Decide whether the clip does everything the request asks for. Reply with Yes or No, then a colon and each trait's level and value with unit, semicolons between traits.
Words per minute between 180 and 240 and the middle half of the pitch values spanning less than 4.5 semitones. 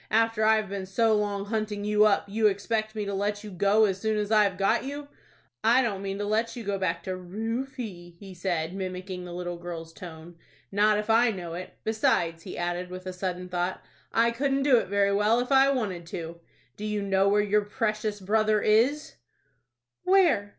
Yes: average, 200 wpm; average, 3.1 semitones